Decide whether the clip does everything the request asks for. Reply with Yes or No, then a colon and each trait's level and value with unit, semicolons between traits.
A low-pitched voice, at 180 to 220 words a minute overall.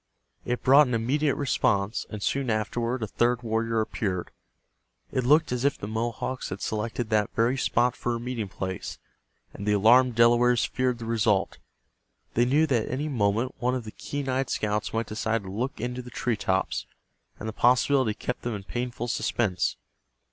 Yes: low, 120 Hz; average, 185 wpm